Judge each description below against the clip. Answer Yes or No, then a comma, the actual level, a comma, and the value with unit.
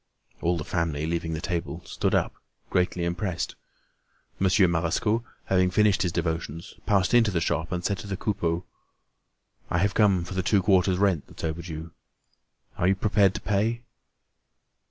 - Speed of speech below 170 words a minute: Yes, average, 160 wpm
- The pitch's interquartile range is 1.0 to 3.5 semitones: Yes, average, 3.1 semitones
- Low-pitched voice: Yes, very low, 90 Hz